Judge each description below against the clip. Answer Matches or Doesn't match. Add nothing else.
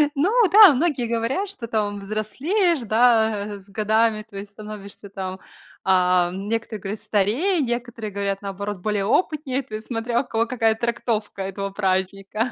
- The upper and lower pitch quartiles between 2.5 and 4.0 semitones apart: Matches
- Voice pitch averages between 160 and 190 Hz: Doesn't match